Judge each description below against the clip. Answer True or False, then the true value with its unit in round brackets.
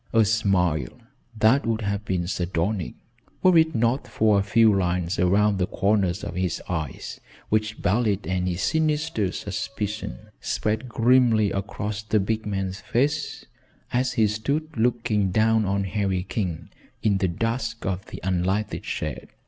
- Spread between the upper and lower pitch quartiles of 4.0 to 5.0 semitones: False (3.1 semitones)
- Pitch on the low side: True (105 Hz)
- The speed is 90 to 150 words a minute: True (145 wpm)